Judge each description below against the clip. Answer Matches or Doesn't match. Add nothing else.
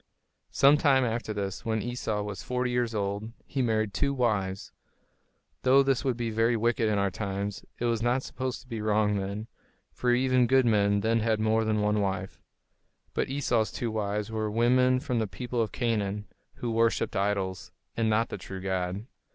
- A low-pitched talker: Matches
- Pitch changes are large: Doesn't match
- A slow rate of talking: Doesn't match